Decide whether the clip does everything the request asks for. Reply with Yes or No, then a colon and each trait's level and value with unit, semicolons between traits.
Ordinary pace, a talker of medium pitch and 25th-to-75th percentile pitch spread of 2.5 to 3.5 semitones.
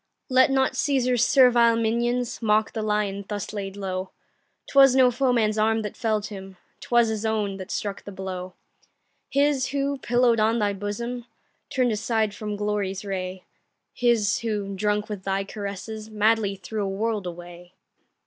No: average, 155 wpm; high, 215 Hz; average, 3.1 semitones